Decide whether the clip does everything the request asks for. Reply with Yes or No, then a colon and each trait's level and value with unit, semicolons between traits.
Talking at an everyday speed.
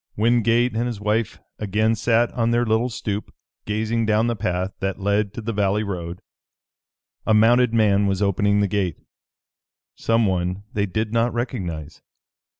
Yes: average, 150 wpm